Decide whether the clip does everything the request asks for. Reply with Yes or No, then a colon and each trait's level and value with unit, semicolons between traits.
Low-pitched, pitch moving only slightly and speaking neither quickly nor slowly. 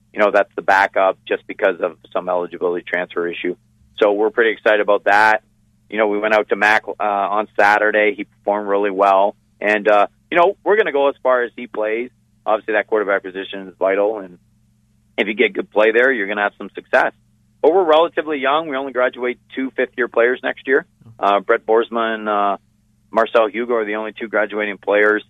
No: low, 110 Hz; narrow, 2.2 semitones; fast, 215 wpm